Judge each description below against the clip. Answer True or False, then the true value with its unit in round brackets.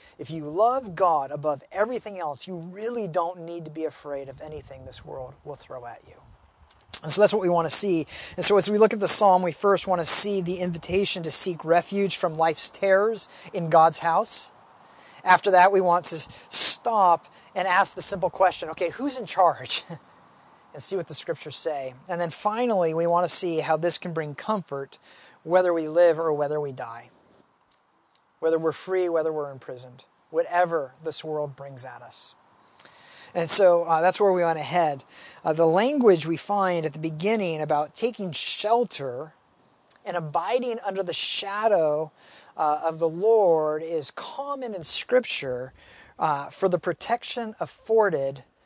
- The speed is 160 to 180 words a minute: True (175 wpm)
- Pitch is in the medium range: True (175 Hz)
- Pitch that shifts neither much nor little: True (3.9 semitones)